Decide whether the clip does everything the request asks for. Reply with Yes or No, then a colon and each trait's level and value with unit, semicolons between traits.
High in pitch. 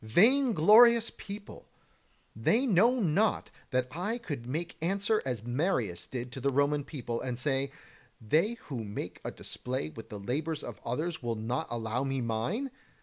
No: medium, 140 Hz